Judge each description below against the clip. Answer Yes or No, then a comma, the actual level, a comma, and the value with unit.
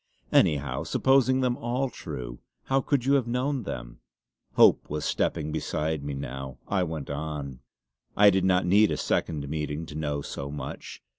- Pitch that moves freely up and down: Yes, wide, 8.8 semitones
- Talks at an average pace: Yes, average, 165 wpm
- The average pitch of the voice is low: Yes, very low, 80 Hz